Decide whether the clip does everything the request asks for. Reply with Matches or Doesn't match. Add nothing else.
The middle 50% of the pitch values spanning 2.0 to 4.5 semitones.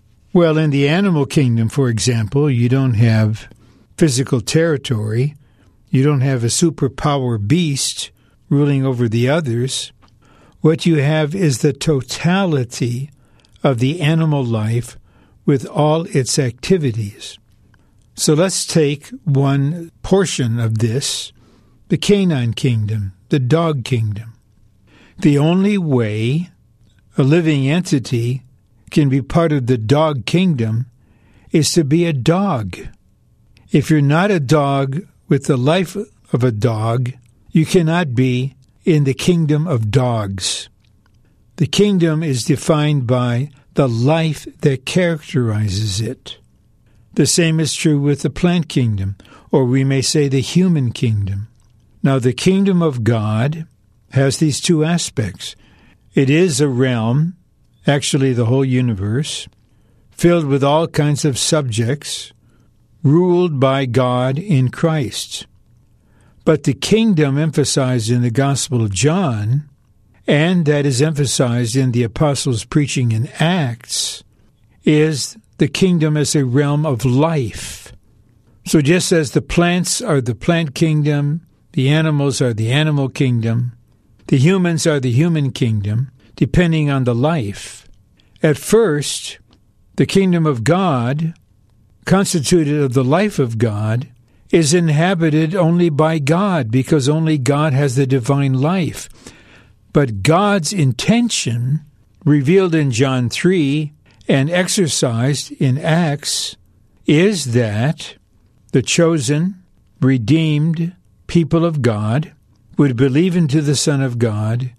Doesn't match